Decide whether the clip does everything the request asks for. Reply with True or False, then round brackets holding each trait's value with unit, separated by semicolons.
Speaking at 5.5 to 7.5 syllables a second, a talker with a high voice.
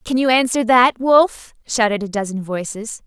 False (4.6 syllables/s; 235 Hz)